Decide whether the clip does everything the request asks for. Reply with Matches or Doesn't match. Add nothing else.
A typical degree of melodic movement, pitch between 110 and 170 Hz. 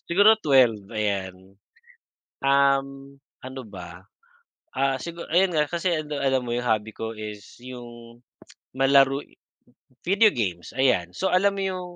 Doesn't match